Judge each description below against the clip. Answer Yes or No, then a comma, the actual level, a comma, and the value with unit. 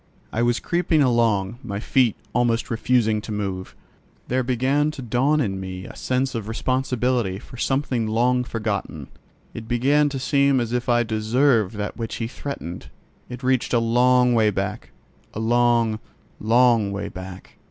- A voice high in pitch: No, low, 120 Hz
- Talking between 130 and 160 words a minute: Yes, average, 155 wpm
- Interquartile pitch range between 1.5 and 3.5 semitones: Yes, average, 2.8 semitones